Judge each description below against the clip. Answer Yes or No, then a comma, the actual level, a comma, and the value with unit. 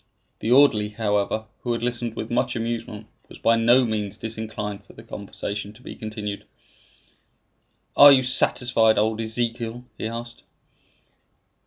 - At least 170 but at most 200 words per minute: No, average, 140 wpm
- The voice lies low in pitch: Yes, low, 115 Hz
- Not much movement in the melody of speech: Yes, narrow, 2.0 semitones